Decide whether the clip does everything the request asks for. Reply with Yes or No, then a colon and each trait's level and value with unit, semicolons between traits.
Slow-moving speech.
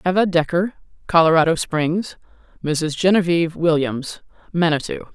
Yes: slow, 95 wpm